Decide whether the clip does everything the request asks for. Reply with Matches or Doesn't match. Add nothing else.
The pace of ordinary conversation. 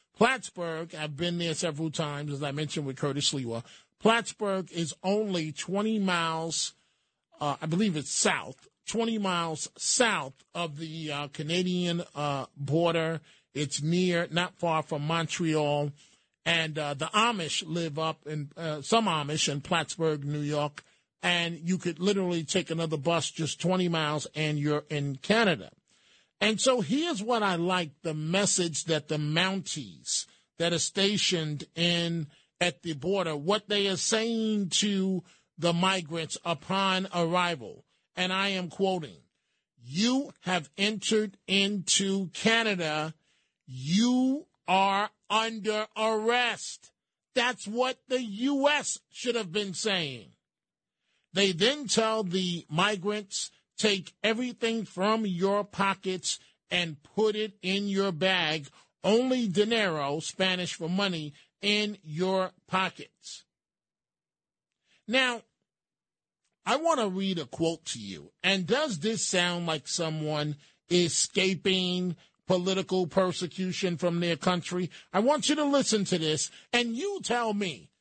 Doesn't match